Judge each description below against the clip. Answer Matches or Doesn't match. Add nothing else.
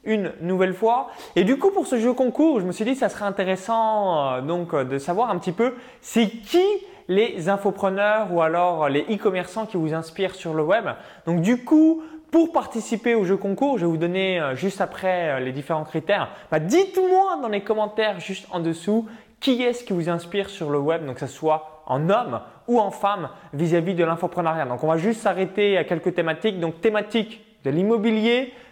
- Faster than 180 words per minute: Matches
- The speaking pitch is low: Doesn't match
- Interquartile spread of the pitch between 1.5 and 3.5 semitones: Doesn't match